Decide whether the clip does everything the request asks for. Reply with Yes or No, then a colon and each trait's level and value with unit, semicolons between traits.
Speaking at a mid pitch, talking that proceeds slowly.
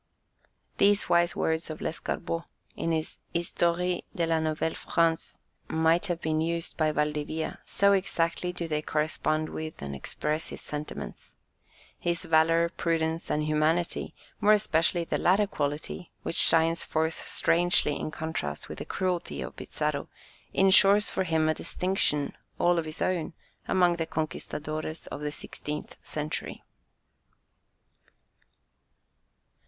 Yes: medium, 165 Hz; slow, 130 wpm